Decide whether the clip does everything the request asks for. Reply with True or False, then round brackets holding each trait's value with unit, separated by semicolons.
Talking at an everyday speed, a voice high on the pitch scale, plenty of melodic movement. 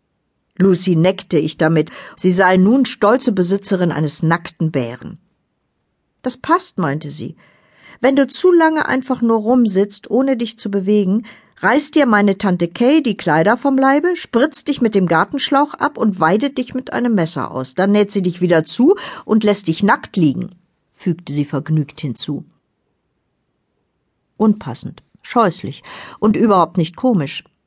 True (150 wpm; 200 Hz; 6.9 semitones)